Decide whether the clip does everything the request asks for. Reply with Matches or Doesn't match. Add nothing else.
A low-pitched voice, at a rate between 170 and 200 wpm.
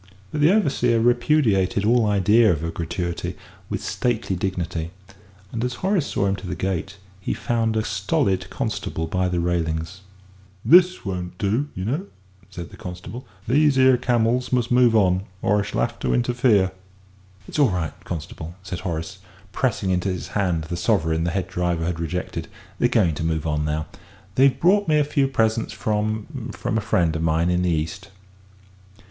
Matches